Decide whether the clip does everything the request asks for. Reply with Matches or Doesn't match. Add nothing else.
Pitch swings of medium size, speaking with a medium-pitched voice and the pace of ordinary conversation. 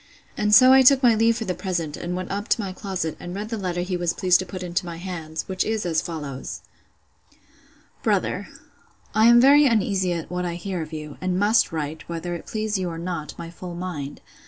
Doesn't match